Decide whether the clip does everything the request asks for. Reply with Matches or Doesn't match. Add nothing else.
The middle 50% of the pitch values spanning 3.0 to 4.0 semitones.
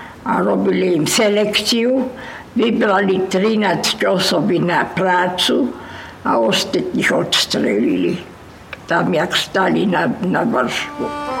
Matches